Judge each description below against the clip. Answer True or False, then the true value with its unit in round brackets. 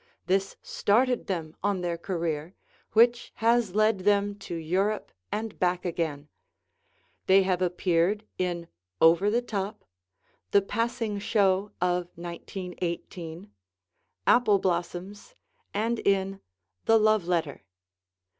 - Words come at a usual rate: False (110 wpm)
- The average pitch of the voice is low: False (190 Hz)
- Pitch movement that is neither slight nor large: True (3.4 semitones)